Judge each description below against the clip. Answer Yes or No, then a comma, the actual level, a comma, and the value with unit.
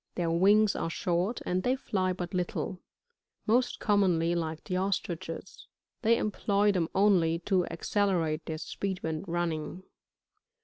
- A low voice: No, medium, 180 Hz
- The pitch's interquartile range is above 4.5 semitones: No, average, 3.4 semitones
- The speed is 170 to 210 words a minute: No, slow, 135 wpm